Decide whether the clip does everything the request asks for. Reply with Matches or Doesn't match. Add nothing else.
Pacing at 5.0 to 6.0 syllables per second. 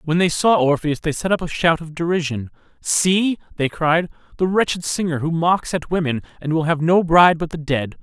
Matches